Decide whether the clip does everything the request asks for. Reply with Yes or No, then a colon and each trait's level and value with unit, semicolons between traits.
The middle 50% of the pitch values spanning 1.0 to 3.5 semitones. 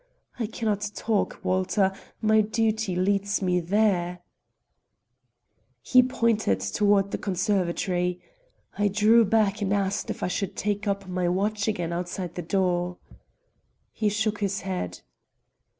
Yes: average, 2.8 semitones